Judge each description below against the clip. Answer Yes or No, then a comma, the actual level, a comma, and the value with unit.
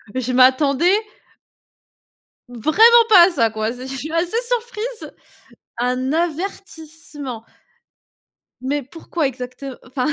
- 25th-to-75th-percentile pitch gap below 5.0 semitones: No, wide, 5.5 semitones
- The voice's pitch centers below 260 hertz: No, very high, 290 Hz